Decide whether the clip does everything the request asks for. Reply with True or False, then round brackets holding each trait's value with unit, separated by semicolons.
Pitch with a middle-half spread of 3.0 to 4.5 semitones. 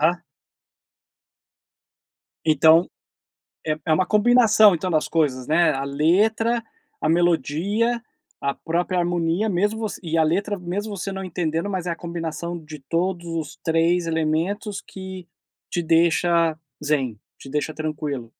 True (3.3 semitones)